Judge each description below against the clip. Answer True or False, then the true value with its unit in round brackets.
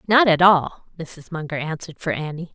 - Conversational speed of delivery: True (190 wpm)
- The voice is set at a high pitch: False (165 Hz)